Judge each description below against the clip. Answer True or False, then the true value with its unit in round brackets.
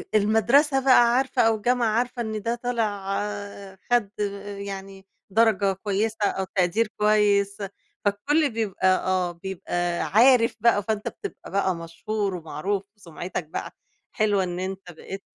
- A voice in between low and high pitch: False (205 Hz)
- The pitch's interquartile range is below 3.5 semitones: True (3.1 semitones)